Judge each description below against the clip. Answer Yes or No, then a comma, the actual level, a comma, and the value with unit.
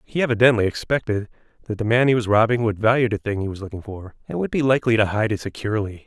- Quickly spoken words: Yes, fast, 245 wpm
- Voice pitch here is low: Yes, low, 110 Hz